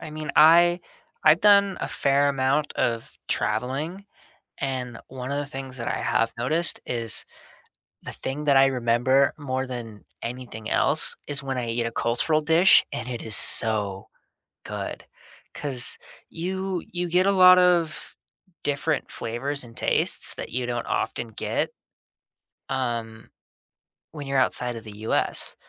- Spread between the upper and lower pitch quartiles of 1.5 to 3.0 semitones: No, average, 4.6 semitones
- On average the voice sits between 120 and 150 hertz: Yes, low, 135 Hz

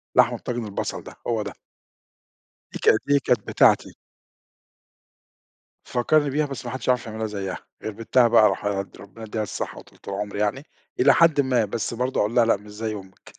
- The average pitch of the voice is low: Yes, low, 115 Hz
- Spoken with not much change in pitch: No, average, 3.4 semitones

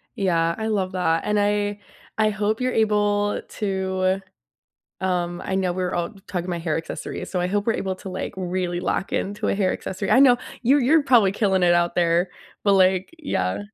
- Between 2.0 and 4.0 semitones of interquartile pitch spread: Yes, narrow, 2.6 semitones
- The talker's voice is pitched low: No, high, 190 Hz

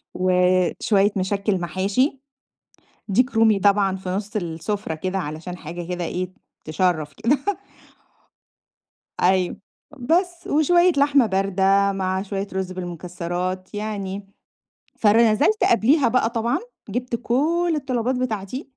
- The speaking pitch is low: No, high, 200 Hz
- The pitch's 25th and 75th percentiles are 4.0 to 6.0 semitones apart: Yes, average, 4.7 semitones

